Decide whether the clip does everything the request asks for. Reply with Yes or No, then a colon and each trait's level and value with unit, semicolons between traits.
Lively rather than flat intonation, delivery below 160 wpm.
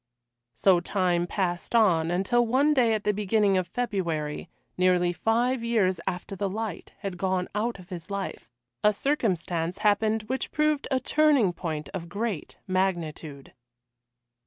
No: average, 4.3 semitones; average, 145 wpm